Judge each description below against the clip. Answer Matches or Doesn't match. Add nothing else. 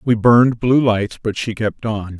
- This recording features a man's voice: Matches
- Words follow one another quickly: Matches